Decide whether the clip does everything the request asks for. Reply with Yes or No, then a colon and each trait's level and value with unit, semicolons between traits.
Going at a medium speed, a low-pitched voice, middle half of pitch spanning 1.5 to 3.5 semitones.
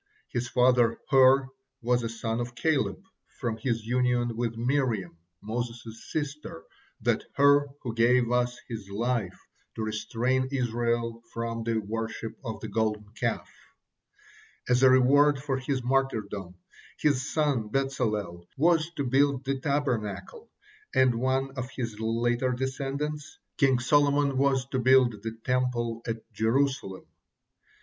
No: slow, 130 wpm; low, 125 Hz; average, 2.9 semitones